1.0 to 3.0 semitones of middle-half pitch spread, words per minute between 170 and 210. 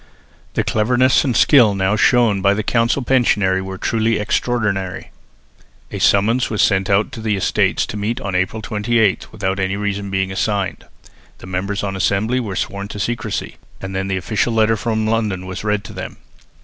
Yes: average, 2.7 semitones; average, 180 wpm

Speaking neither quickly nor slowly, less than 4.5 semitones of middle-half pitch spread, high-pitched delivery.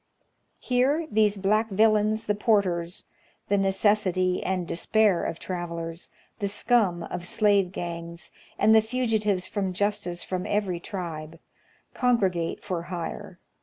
No: slow, 130 wpm; average, 3.4 semitones; high, 195 Hz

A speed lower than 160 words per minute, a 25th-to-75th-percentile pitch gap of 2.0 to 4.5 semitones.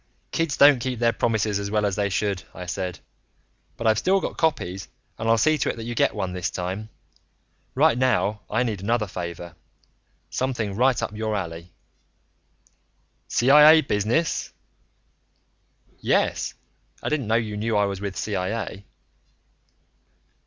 Yes: average, 150 wpm; average, 3.7 semitones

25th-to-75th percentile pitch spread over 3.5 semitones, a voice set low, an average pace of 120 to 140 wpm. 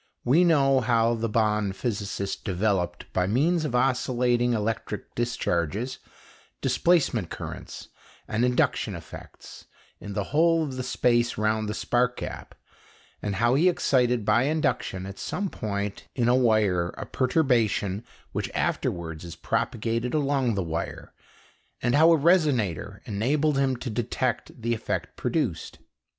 Yes: average, 4.3 semitones; low, 120 Hz; slow, 135 wpm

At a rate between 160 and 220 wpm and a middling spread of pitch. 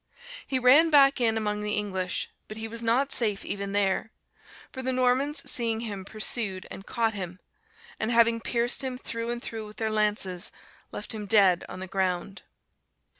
Yes: average, 175 wpm; average, 3.2 semitones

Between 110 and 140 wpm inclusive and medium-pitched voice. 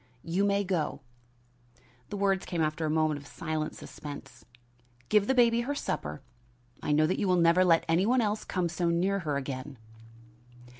No: average, 180 wpm; medium, 170 Hz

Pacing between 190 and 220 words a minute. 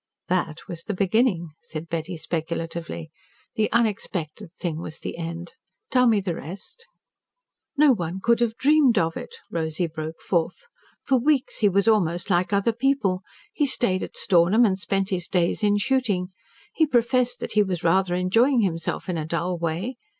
No: average, 170 wpm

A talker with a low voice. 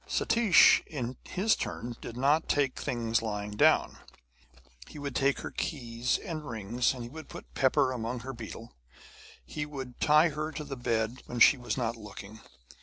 Yes: low, 125 Hz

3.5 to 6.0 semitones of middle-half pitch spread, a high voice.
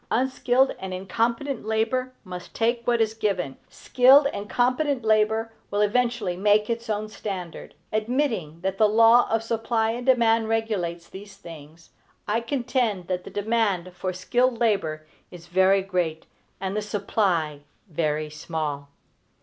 Yes: average, 4.3 semitones; high, 215 Hz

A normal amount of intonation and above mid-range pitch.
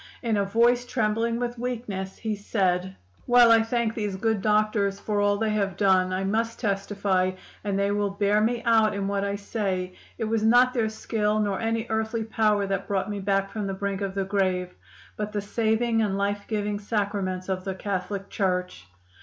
No: narrow, 2.3 semitones; high, 205 Hz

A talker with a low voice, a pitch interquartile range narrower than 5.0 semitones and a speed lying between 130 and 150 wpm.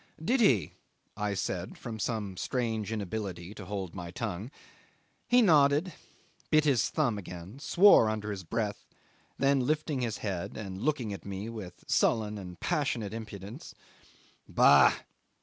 No: low, 110 Hz; wide, 5.4 semitones; average, 140 wpm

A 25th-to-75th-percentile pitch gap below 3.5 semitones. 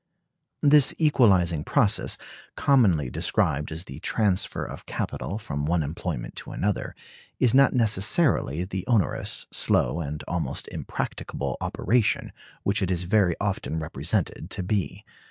No: wide, 5.6 semitones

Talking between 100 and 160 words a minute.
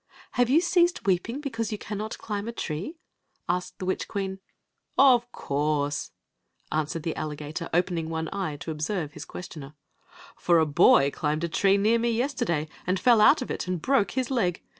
No: average, 185 wpm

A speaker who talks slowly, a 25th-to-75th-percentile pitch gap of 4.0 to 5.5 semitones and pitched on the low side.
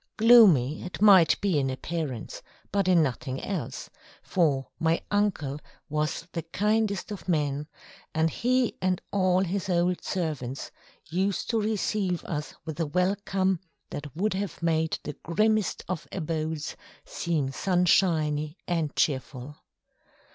No: slow, 130 wpm; average, 4.3 semitones; medium, 170 Hz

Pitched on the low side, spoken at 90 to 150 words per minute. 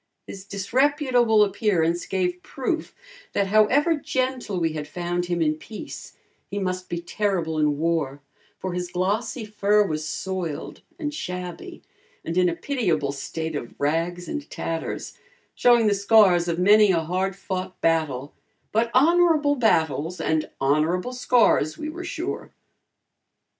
No: medium, 185 Hz; average, 140 wpm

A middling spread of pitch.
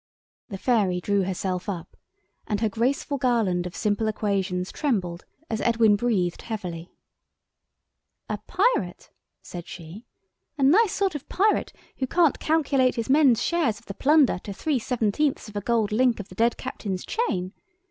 No: wide, 5.8 semitones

